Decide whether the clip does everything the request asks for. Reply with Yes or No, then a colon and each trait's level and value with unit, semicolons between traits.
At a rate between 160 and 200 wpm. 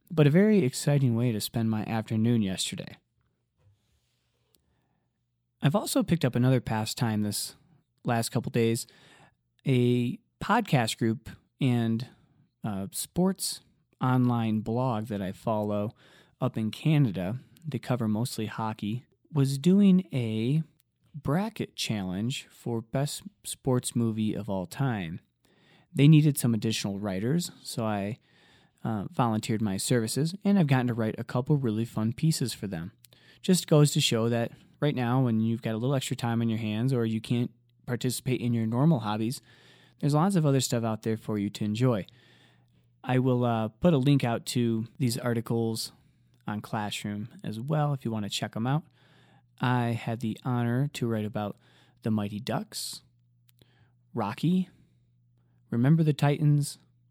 No: average, 150 wpm